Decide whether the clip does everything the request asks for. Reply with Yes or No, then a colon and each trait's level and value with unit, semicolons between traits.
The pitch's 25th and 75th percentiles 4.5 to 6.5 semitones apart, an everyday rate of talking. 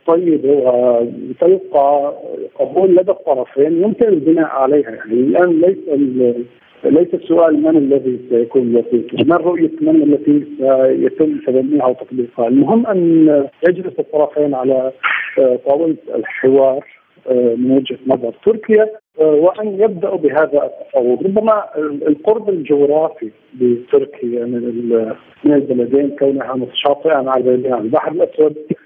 Yes: wide, 5.5 semitones; average, 105 wpm